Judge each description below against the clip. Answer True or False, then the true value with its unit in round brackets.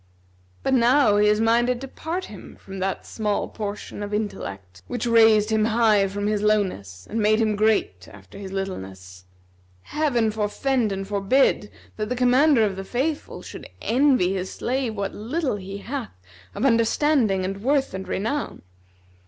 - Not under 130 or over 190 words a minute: True (160 wpm)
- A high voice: True (215 Hz)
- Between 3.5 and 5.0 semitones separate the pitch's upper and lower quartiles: True (4.0 semitones)